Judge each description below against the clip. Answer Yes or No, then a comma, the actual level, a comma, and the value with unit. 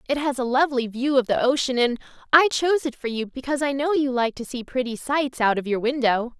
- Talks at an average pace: No, fast, 255 wpm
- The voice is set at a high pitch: Yes, very high, 260 Hz